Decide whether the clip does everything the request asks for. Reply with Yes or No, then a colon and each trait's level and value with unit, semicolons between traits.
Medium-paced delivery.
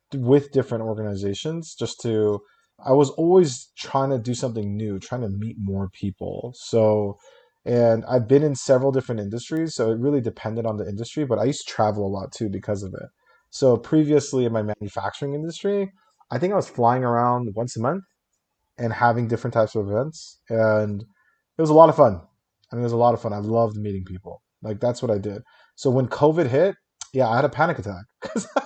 No: fast, 210 wpm